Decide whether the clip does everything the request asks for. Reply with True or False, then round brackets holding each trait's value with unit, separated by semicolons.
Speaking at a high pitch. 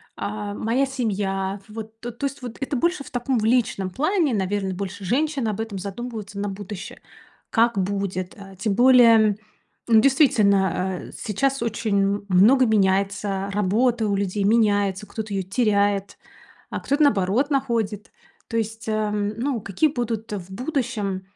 True (215 Hz)